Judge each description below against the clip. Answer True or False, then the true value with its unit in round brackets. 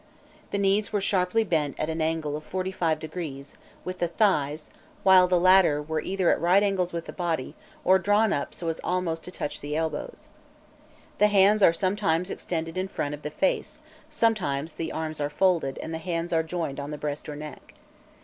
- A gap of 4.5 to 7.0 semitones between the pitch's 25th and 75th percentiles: False (3.7 semitones)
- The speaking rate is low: False (190 wpm)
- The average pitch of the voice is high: False (170 Hz)